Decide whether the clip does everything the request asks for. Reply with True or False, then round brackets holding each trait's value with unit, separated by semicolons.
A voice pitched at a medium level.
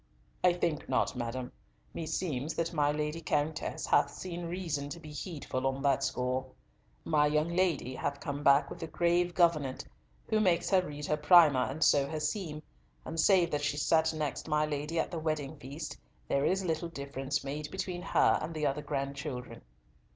True (150 Hz)